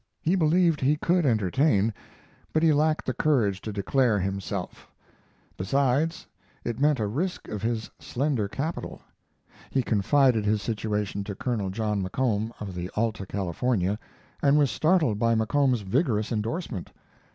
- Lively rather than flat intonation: Yes, wide, 5.9 semitones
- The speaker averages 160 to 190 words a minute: No, average, 140 wpm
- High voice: No, low, 115 Hz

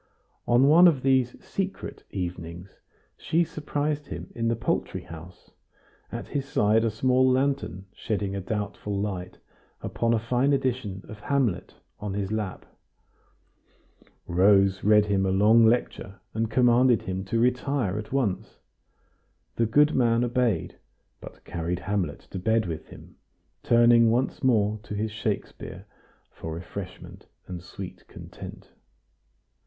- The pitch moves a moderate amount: Yes, average, 4.6 semitones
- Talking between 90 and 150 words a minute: Yes, slow, 135 wpm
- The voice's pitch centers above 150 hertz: No, low, 110 Hz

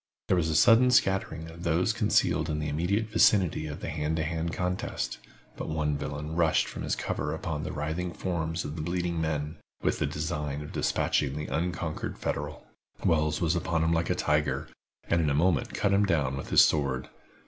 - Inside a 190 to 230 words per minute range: Yes, average, 200 wpm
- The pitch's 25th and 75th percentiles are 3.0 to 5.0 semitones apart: No, narrow, 2.5 semitones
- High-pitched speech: No, very low, 80 Hz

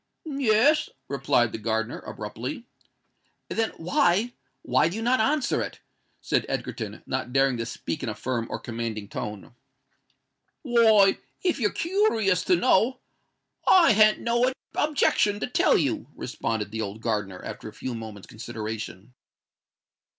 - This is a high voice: No, medium, 140 Hz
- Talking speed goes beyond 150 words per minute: No, slow, 135 wpm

